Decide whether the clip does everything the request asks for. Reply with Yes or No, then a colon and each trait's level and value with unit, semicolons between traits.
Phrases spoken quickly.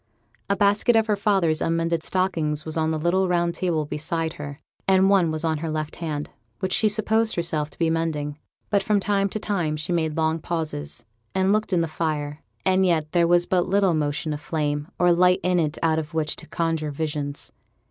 Yes: fast, 210 wpm